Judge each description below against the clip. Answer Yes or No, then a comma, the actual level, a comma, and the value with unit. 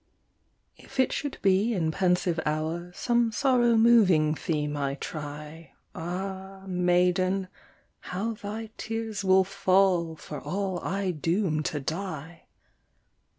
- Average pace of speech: No, slow, 115 wpm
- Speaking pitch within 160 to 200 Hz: Yes, medium, 185 Hz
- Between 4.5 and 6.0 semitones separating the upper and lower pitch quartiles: No, average, 3.8 semitones